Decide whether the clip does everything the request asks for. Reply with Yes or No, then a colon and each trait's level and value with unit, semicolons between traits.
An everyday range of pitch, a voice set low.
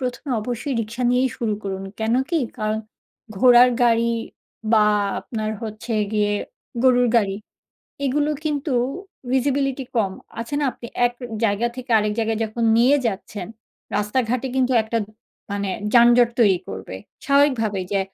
No: average, 3.0 semitones; high, 235 Hz